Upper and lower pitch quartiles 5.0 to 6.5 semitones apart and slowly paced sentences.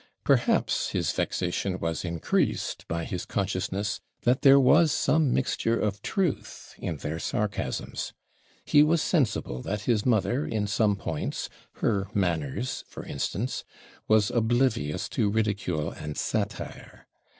Yes: wide, 5.6 semitones; slow, 130 wpm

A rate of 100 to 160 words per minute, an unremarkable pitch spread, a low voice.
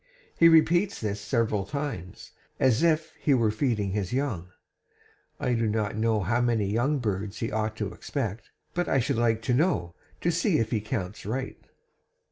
No: average, 175 wpm; average, 4.6 semitones; low, 115 Hz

